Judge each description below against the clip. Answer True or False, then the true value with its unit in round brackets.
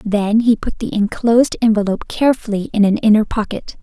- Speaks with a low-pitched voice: False (215 Hz)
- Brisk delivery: False (175 wpm)